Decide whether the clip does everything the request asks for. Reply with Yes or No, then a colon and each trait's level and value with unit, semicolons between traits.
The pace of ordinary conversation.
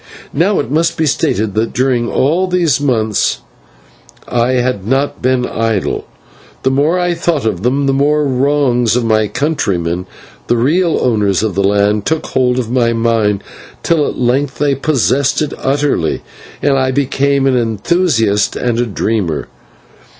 Yes: average, 160 wpm